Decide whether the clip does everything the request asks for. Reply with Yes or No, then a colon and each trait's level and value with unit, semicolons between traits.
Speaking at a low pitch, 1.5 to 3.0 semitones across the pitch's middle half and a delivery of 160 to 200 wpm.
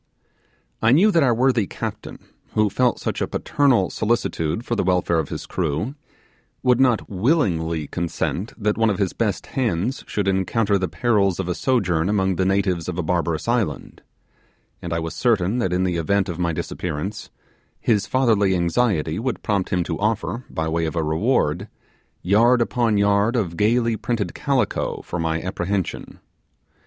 No: low, 100 Hz; average, 5.1 semitones; average, 170 wpm